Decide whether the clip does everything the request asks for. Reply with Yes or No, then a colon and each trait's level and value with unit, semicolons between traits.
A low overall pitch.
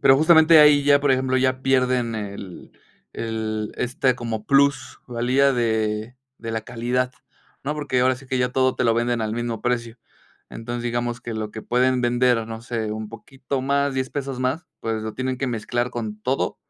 Yes: low, 125 Hz